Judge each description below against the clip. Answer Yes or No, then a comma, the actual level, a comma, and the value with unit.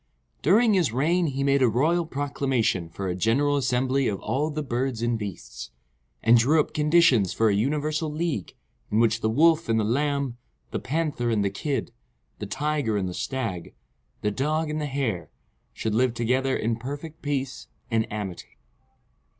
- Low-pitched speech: Yes, low, 130 Hz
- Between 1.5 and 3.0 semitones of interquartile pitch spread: No, average, 5.1 semitones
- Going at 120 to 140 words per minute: No, average, 175 wpm